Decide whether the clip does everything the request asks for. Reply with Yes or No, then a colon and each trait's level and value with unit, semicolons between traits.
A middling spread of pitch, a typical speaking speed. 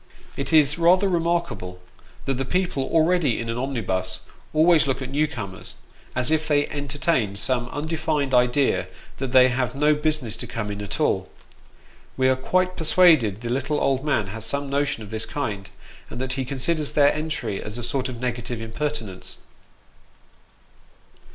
Yes: average, 4.5 semitones; average, 165 wpm